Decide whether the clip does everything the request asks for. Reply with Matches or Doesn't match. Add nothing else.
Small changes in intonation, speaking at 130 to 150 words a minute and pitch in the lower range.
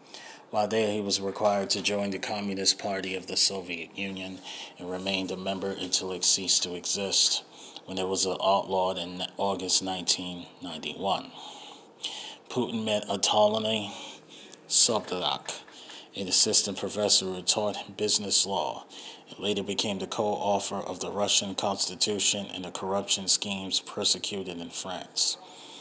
Matches